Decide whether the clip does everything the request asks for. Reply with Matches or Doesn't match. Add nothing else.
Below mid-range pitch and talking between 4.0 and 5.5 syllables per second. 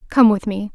Doesn't match